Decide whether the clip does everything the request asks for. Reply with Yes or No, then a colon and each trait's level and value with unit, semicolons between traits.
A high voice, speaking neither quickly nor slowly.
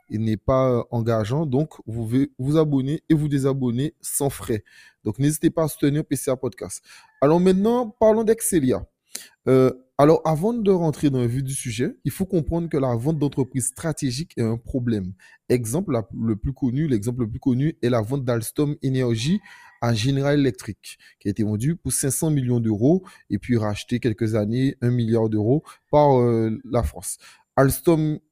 No: low, 135 Hz; average, 175 wpm